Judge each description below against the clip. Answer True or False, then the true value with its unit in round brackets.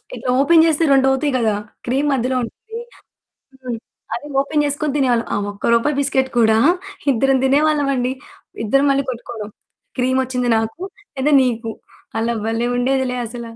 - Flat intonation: False (3.0 semitones)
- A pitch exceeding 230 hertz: True (260 Hz)